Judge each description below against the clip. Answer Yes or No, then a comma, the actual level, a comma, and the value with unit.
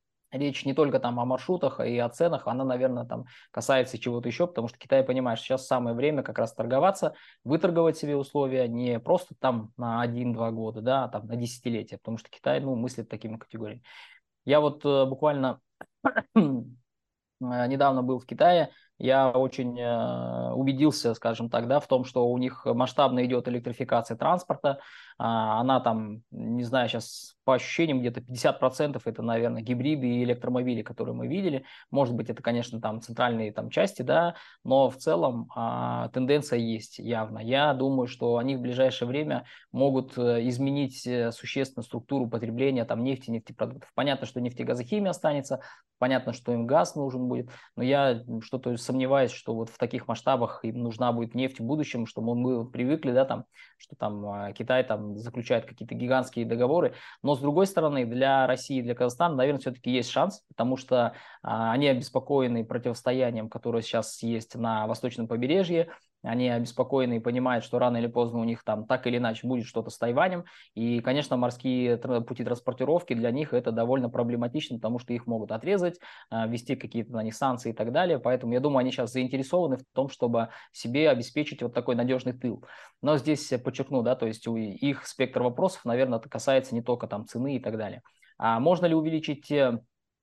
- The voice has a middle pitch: No, low, 125 Hz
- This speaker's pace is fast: Yes, fast, 170 wpm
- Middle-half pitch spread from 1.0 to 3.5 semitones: Yes, narrow, 2.4 semitones